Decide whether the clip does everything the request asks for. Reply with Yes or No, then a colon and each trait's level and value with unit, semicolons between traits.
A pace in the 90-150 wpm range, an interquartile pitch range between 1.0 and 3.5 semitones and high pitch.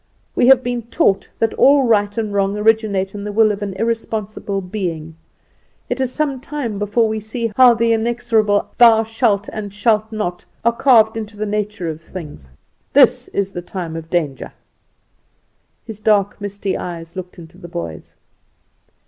No: average, 165 wpm; average, 2.9 semitones; high, 210 Hz